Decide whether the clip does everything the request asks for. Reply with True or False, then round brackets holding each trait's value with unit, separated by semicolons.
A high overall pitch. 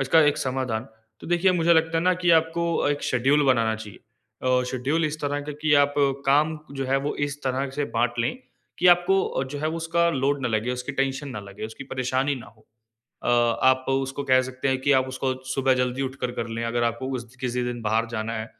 False (130 Hz)